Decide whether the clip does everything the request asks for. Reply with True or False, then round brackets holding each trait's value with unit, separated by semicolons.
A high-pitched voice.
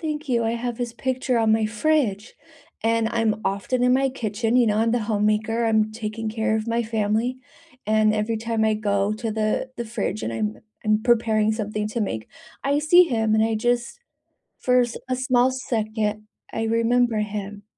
True (225 Hz)